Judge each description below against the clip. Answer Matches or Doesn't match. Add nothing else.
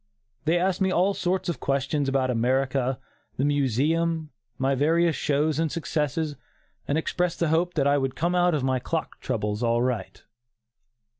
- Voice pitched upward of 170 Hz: Doesn't match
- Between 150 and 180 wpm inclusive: Matches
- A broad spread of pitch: Doesn't match